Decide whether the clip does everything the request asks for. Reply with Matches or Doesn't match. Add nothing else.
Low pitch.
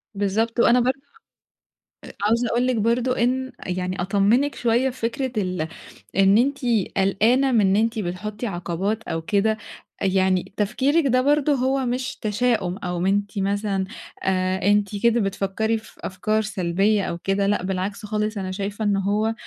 Doesn't match